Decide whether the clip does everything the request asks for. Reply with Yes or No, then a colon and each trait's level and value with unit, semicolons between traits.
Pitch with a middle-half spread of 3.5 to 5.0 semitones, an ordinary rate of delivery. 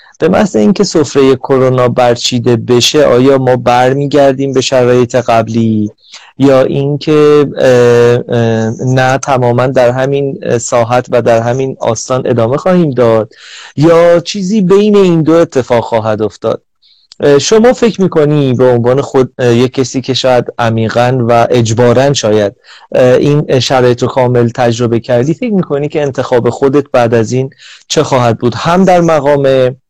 No: average, 3.0 semitones; average, 135 wpm